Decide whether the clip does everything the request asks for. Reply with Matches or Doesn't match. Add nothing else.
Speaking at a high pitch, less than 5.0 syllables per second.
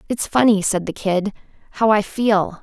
Matches